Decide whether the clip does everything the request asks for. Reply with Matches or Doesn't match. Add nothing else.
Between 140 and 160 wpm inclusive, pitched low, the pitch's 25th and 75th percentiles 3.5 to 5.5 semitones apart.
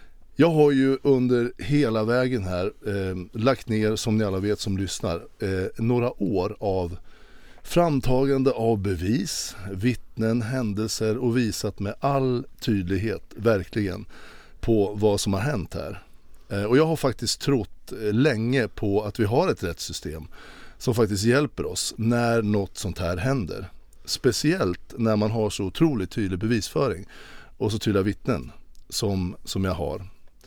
Matches